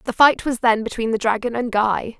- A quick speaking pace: Yes, fast, 245 wpm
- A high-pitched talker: Yes, high, 230 Hz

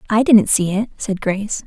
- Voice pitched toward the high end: Yes, high, 205 Hz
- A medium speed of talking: No, fast, 215 wpm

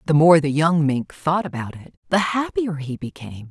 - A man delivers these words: No, female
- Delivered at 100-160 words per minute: No, fast, 205 wpm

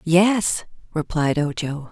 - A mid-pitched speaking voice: Yes, medium, 160 Hz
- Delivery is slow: Yes, slow, 95 wpm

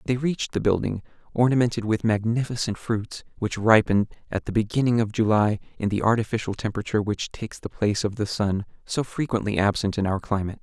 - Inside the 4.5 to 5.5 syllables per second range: No, 6.2 syllables/s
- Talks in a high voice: No, low, 110 Hz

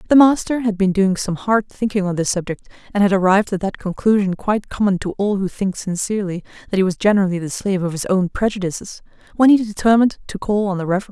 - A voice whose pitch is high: Yes, high, 200 Hz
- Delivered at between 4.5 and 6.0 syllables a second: No, 6.4 syllables/s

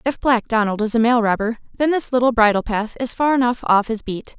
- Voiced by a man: No, female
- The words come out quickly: Yes, fast, 245 wpm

